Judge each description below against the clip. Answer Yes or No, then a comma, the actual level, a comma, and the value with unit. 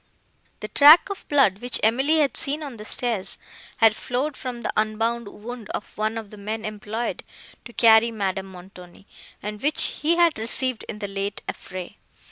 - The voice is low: No, high, 225 Hz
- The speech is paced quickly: No, average, 175 wpm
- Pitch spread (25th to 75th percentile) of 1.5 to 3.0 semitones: No, average, 3.7 semitones